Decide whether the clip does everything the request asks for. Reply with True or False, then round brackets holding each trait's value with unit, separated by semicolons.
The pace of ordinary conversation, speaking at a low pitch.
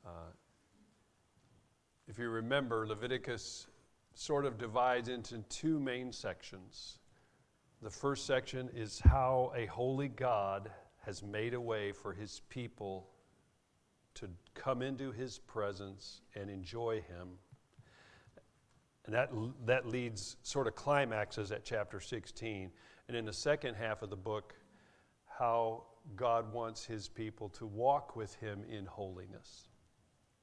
False (125 wpm; 115 Hz)